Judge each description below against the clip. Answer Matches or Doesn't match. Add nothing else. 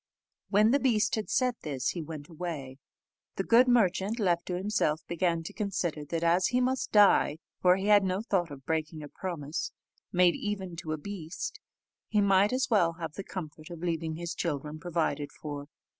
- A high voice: Doesn't match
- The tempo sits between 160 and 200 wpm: Matches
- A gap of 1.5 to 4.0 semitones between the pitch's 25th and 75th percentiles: Doesn't match